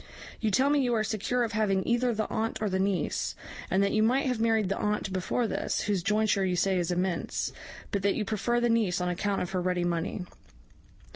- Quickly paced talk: Yes, fast, 225 wpm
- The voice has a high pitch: Yes, high, 205 Hz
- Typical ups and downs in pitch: Yes, average, 3.3 semitones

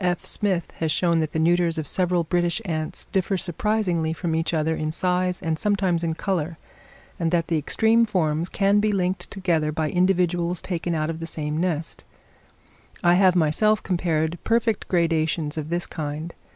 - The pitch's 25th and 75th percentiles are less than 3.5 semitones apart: Yes, narrow, 2.4 semitones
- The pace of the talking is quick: No, average, 175 wpm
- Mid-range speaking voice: Yes, medium, 170 Hz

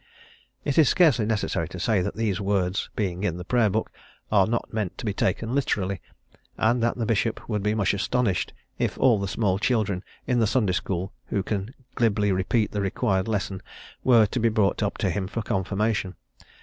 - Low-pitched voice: Yes, low, 105 Hz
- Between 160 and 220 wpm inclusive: Yes, average, 195 wpm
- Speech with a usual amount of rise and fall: Yes, average, 3.0 semitones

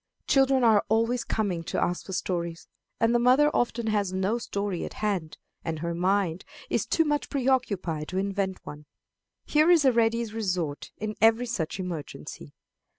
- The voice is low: No, high, 205 Hz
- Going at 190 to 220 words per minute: No, average, 165 wpm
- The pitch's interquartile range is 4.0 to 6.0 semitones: Yes, average, 5.1 semitones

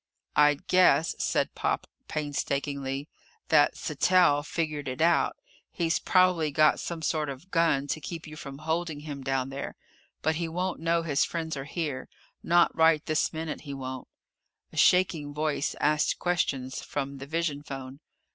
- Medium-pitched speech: Yes, medium, 150 Hz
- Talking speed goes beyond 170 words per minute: No, average, 155 wpm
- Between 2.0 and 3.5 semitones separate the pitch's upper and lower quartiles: Yes, average, 3.0 semitones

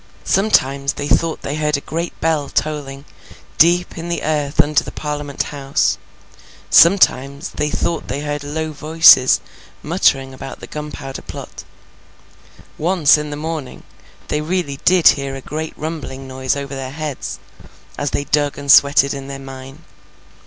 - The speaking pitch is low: No, medium, 145 Hz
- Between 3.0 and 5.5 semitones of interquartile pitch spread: No, narrow, 2.4 semitones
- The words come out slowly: No, average, 155 wpm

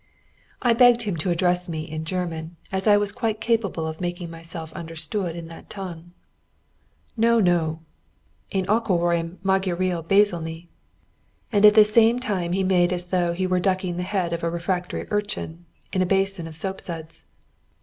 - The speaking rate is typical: Yes, average, 165 wpm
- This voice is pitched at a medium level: Yes, medium, 180 Hz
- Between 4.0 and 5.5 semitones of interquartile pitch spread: No, average, 2.9 semitones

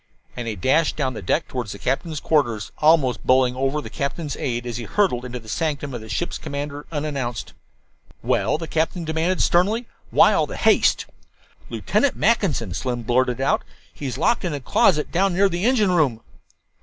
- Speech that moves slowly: No, average, 180 wpm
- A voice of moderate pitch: Yes, medium, 145 Hz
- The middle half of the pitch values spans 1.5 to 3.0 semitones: No, average, 5.2 semitones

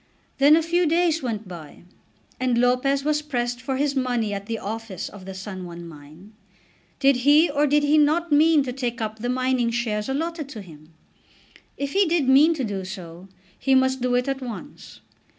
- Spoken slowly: No, average, 195 wpm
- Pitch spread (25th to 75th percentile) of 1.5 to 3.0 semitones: No, wide, 5.5 semitones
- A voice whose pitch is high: Yes, very high, 255 Hz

